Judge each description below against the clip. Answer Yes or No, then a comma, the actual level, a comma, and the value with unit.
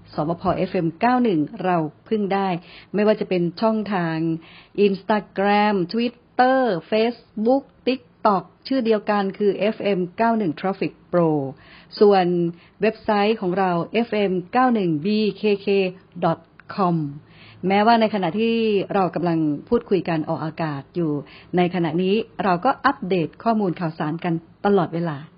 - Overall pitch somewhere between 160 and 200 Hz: Yes, high, 190 Hz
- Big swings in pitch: No, average, 4.0 semitones